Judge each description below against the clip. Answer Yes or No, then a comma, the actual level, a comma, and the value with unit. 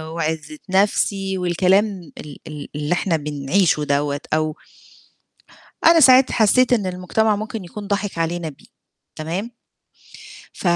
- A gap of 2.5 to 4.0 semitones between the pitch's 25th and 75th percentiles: No, average, 4.9 semitones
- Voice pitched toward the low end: No, medium, 180 Hz